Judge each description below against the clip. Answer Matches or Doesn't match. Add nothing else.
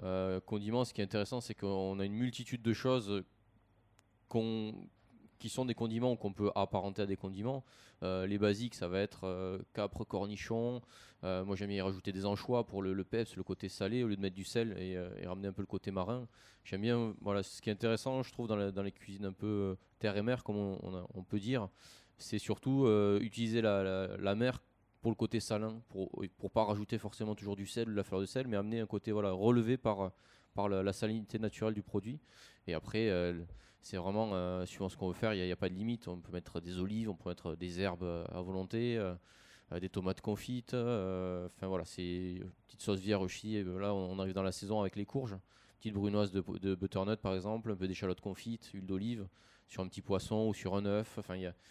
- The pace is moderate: Doesn't match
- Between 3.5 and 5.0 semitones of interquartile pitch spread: Doesn't match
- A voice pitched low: Matches